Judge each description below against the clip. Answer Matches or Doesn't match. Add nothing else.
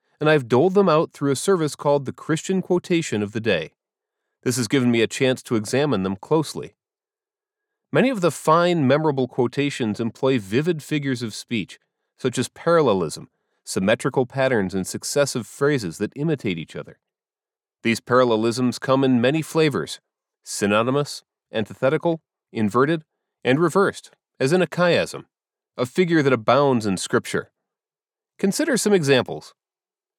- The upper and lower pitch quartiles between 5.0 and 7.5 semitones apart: Matches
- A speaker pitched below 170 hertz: Matches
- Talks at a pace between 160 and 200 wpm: Doesn't match